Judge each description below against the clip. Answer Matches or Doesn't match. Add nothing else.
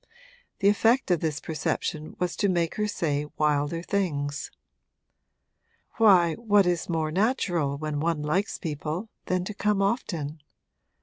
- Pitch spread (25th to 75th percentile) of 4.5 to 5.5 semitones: Matches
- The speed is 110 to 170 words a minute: Matches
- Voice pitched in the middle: Matches